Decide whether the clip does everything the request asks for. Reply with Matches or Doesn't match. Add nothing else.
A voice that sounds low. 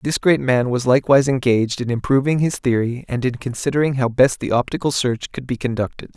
Matches